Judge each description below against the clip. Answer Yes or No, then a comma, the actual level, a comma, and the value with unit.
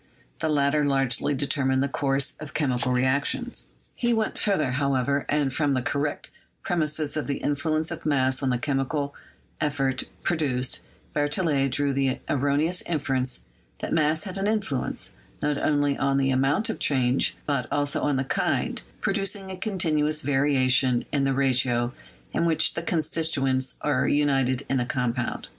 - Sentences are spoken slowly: No, average, 160 wpm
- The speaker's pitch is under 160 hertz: Yes, medium, 140 Hz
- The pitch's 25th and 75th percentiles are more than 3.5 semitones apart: No, narrow, 2.6 semitones